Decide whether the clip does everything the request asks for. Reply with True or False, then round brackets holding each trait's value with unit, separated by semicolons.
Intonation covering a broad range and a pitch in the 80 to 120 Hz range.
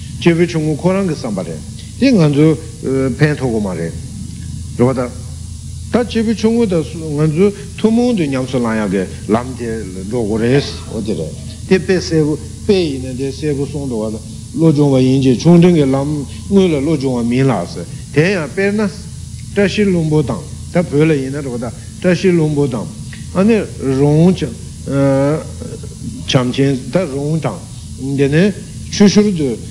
False (5.8 semitones; 140 Hz)